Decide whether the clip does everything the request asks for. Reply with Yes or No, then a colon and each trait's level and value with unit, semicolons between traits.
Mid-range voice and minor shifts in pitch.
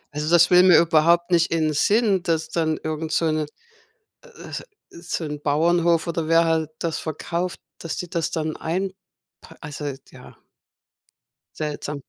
Yes: medium, 165 Hz; narrow, 1.7 semitones